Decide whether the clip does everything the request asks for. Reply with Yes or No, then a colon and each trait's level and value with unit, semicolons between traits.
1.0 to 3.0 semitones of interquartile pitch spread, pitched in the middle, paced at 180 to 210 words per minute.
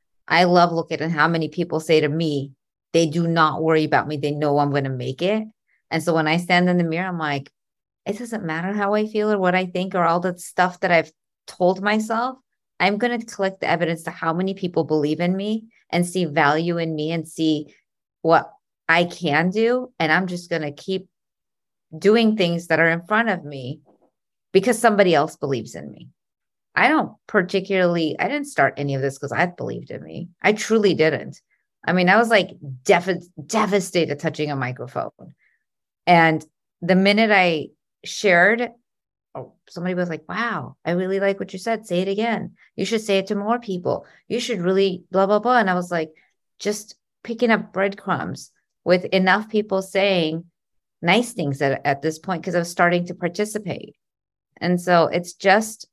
No: average, 3.9 semitones; medium, 180 Hz; average, 195 wpm